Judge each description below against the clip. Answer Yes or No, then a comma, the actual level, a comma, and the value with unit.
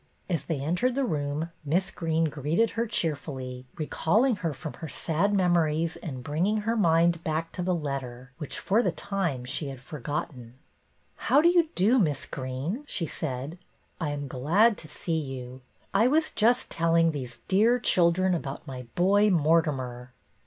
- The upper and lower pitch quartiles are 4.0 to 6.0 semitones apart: Yes, wide, 5.4 semitones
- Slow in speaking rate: No, average, 175 wpm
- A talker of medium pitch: Yes, medium, 165 Hz